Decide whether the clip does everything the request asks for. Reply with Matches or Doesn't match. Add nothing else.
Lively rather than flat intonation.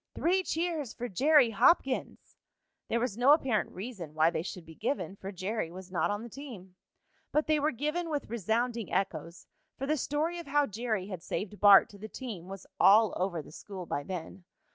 Matches